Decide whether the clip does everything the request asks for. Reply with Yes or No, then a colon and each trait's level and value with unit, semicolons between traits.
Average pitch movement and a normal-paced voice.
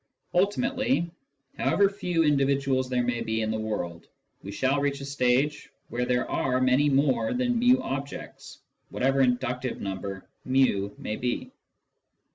Yes: average, 3.3 semitones; average, 145 wpm